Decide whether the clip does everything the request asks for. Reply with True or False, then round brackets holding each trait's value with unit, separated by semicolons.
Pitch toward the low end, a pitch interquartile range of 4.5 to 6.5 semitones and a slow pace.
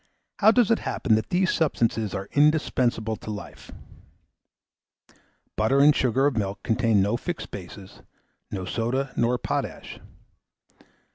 True (120 Hz; 5.1 semitones; 130 wpm)